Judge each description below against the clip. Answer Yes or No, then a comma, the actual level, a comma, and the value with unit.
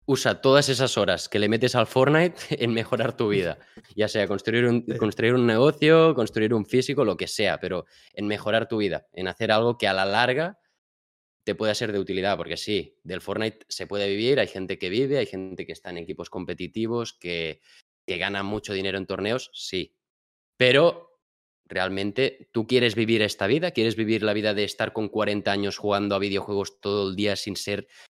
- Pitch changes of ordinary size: Yes, average, 3.1 semitones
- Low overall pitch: Yes, low, 110 Hz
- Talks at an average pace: No, fast, 200 wpm